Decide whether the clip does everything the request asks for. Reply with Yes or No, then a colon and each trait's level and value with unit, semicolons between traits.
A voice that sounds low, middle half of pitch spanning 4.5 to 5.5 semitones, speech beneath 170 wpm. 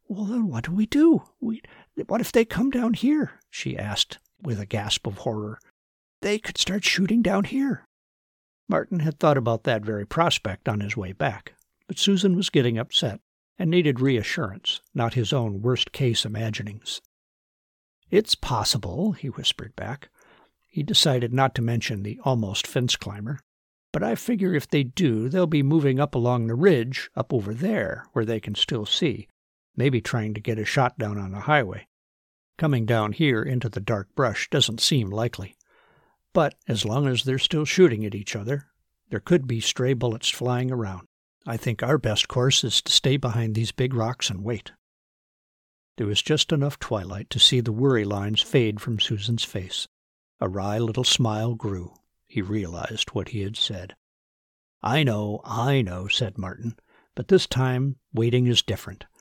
No: low, 120 Hz; average, 5.0 semitones; average, 175 wpm